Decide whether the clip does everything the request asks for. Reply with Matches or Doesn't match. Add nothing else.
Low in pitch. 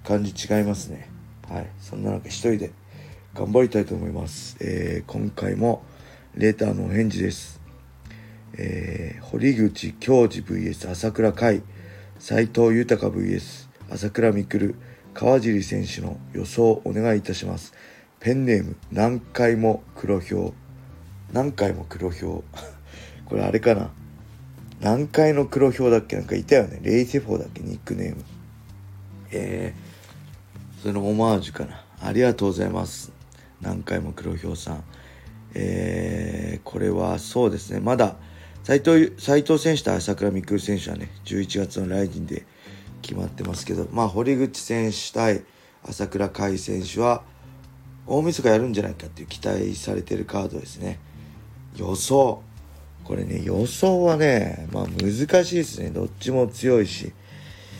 Matches